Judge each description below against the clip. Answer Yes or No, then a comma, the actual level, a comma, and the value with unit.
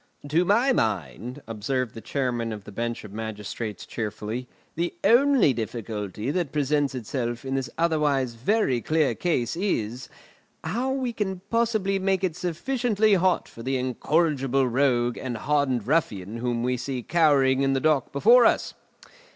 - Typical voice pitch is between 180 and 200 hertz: No, low, 135 Hz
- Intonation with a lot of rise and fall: Yes, wide, 6.8 semitones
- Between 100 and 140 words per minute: No, average, 150 wpm